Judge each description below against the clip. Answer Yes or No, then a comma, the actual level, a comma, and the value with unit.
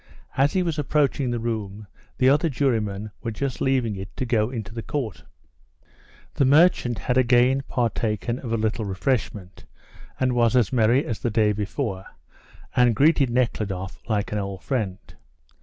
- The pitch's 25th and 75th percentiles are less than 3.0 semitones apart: No, average, 3.6 semitones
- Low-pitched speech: Yes, low, 120 Hz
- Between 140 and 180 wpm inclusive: Yes, average, 160 wpm